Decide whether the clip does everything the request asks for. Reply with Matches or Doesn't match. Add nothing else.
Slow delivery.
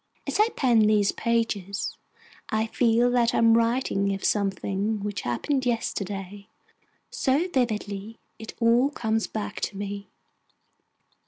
Matches